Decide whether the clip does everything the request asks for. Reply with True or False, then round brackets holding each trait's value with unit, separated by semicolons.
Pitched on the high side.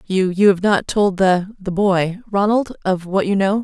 True (195 Hz)